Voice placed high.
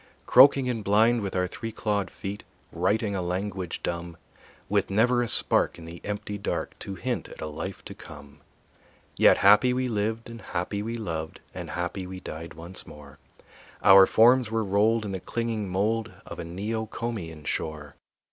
No: low, 100 Hz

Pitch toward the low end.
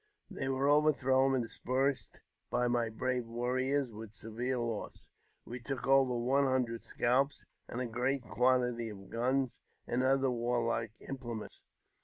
Yes: low, 125 Hz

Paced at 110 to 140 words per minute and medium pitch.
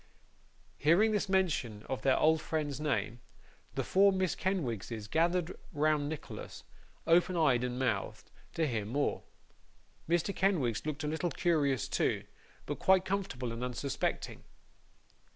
Yes: slow, 135 wpm; medium, 155 Hz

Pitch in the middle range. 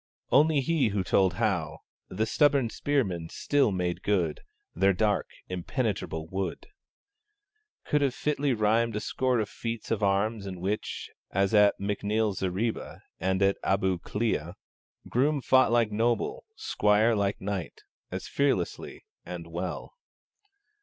No: low, 105 Hz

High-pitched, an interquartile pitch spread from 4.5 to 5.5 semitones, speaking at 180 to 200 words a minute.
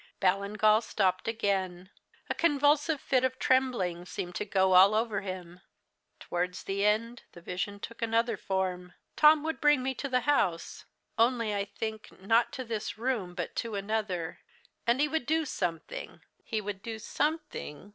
No: high, 215 Hz; average, 5.2 semitones; average, 160 wpm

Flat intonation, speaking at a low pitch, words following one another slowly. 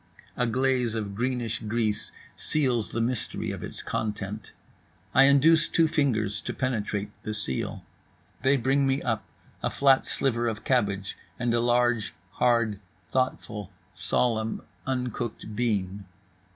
No: average, 3.4 semitones; low, 120 Hz; slow, 130 wpm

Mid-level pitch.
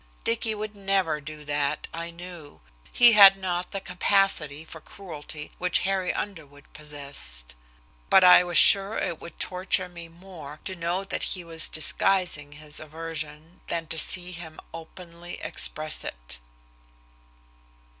Yes: medium, 170 Hz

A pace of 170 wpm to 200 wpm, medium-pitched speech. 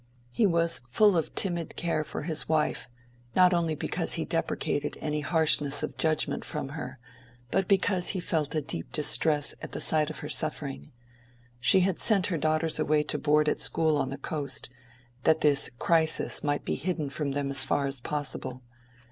Yes: average, 185 wpm; medium, 155 Hz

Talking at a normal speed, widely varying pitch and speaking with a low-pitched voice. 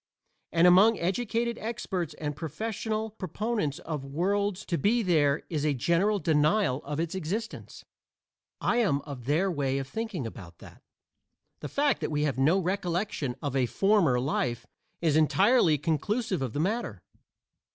No: average, 150 wpm; wide, 6.3 semitones; medium, 170 Hz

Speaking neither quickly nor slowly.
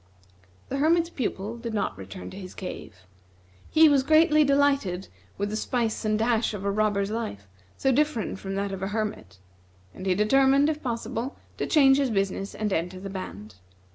Yes: average, 180 wpm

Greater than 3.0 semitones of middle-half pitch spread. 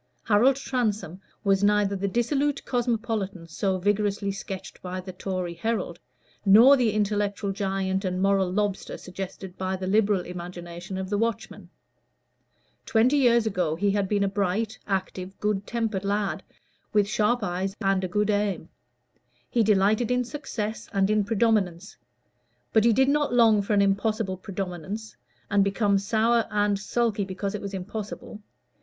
No: narrow, 2.5 semitones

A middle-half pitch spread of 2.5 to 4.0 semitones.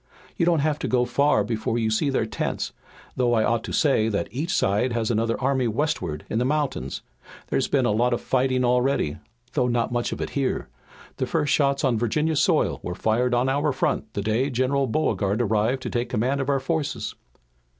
Yes: average, 3.7 semitones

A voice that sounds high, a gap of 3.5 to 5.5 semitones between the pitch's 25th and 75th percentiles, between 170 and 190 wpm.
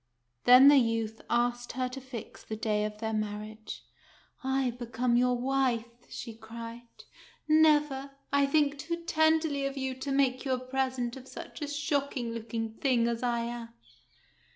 No: very high, 250 Hz; average, 3.0 semitones; average, 175 wpm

